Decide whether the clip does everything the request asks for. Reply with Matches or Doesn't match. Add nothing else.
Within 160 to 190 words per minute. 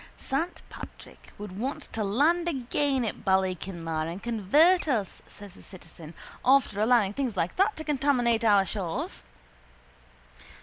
Doesn't match